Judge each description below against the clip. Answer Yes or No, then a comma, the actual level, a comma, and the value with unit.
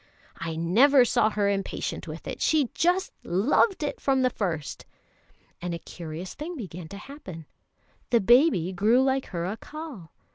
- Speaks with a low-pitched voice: No, high, 215 Hz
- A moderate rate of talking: Yes, average, 155 wpm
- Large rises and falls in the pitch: Yes, wide, 7.8 semitones